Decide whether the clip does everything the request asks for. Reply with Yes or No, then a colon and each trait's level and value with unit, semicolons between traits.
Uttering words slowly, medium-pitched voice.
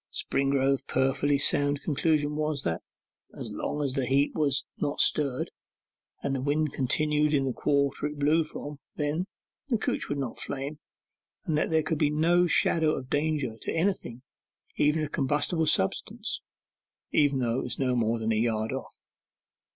No: average, 165 wpm; medium, 145 Hz